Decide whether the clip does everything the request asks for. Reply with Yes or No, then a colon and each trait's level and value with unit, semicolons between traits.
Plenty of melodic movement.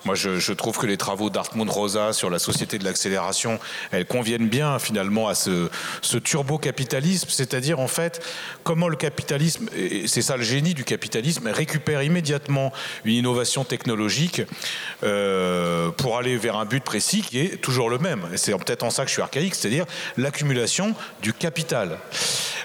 Yes: wide, 6.3 semitones